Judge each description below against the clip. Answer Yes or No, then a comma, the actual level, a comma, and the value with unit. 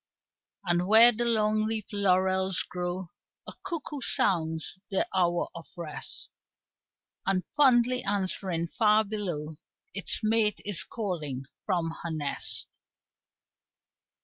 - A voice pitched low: No, high, 190 Hz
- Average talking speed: No, slow, 110 wpm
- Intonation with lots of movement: No, average, 3.9 semitones